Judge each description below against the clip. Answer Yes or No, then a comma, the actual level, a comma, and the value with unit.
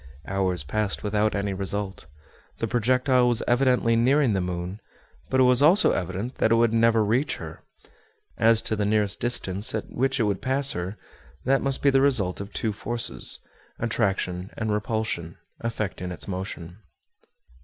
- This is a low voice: Yes, low, 110 Hz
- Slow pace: No, average, 165 wpm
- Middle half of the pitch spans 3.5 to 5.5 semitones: Yes, average, 4.1 semitones